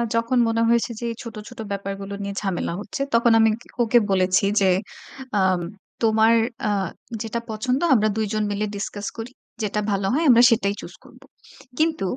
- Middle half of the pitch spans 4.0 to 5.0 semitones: No, average, 2.8 semitones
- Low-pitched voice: No, high, 220 Hz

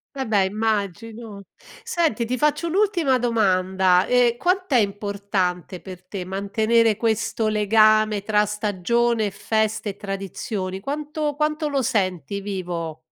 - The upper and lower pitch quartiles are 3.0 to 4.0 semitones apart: Yes, average, 3.5 semitones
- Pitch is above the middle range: Yes, high, 215 Hz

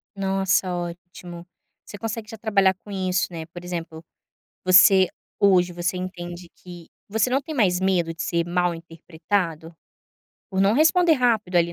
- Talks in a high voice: No, medium, 180 Hz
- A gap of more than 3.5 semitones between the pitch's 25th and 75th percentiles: No, narrow, 2.5 semitones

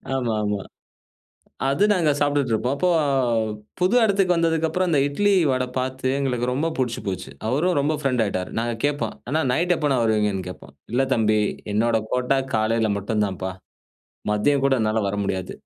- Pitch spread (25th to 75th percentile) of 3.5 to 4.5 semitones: No, wide, 5.4 semitones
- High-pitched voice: No, low, 125 Hz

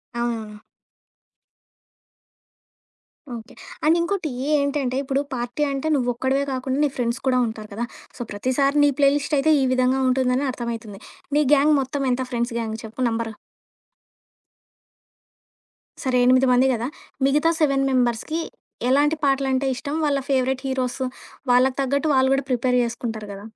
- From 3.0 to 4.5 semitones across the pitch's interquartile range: No, narrow, 2.6 semitones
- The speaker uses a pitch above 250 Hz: Yes, very high, 260 Hz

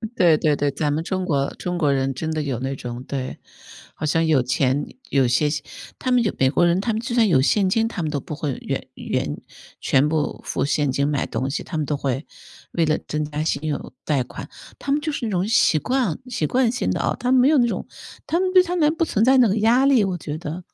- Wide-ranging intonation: Yes, wide, 8.2 semitones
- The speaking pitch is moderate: Yes, medium, 160 Hz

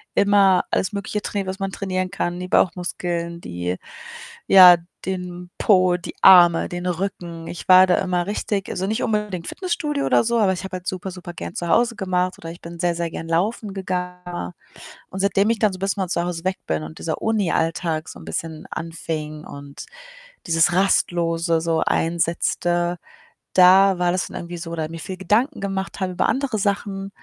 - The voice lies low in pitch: No, medium, 180 Hz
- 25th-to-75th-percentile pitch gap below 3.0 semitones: Yes, narrow, 2.5 semitones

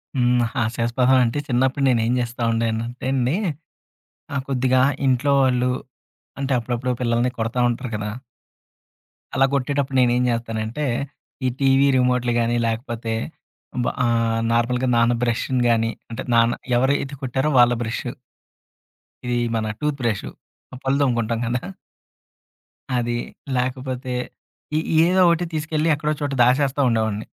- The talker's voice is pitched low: Yes, low, 125 Hz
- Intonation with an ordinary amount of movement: No, narrow, 2.2 semitones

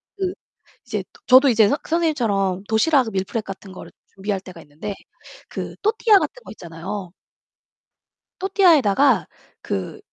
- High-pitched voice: Yes, high, 220 Hz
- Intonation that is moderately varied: No, wide, 9.0 semitones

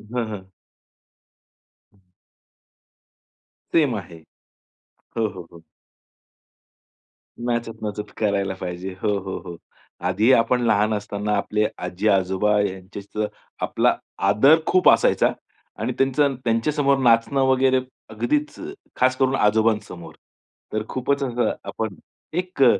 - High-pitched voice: No, low, 110 Hz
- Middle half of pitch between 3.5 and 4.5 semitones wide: Yes, average, 4.2 semitones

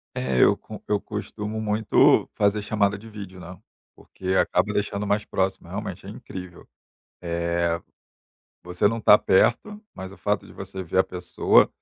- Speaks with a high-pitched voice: No, low, 100 Hz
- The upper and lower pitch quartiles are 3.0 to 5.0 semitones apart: No, narrow, 2.5 semitones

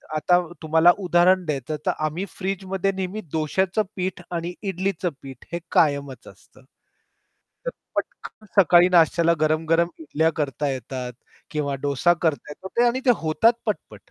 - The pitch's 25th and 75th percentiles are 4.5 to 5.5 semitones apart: No, average, 3.6 semitones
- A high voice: No, medium, 170 Hz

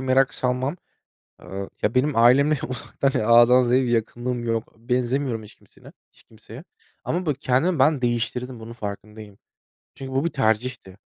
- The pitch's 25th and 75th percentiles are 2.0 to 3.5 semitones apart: Yes, average, 2.7 semitones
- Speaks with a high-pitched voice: No, low, 125 Hz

